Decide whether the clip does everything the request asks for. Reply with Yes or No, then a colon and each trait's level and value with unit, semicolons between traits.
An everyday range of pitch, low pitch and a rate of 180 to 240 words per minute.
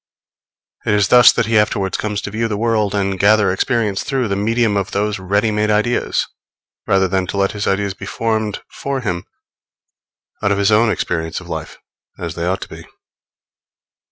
No: narrow, 2.1 semitones; low, 105 Hz; average, 185 wpm